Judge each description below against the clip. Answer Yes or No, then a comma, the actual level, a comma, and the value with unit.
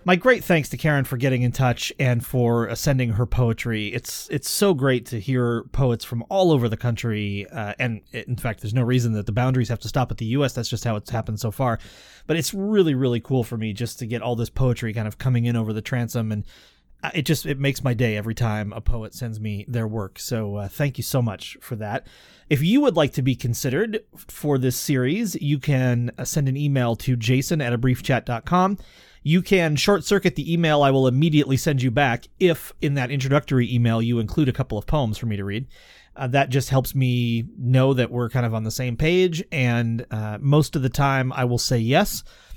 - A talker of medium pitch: No, low, 125 Hz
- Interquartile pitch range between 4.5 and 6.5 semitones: No, average, 3.6 semitones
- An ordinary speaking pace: No, fast, 230 wpm